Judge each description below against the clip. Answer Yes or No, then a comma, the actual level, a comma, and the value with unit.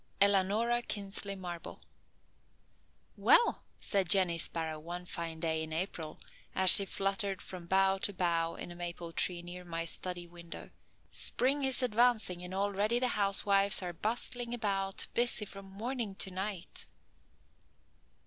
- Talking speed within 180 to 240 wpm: No, average, 140 wpm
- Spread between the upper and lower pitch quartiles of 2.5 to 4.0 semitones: Yes, average, 3.0 semitones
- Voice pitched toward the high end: Yes, high, 195 Hz